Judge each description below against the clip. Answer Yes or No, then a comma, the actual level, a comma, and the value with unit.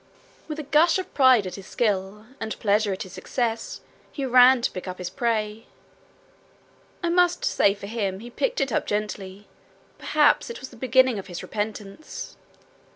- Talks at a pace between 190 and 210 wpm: No, average, 175 wpm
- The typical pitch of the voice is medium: No, high, 225 Hz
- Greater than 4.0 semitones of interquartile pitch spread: Yes, average, 4.7 semitones